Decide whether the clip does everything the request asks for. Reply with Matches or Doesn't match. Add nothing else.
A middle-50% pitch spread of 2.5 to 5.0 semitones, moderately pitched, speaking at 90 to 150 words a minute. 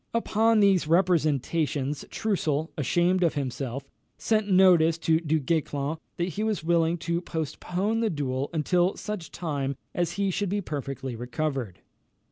Matches